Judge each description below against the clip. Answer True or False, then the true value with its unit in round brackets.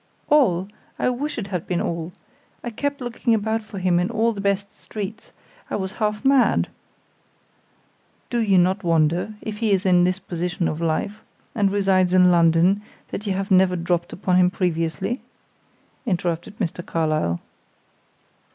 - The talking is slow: False (160 wpm)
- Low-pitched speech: False (190 Hz)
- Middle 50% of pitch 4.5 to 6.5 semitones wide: False (3.4 semitones)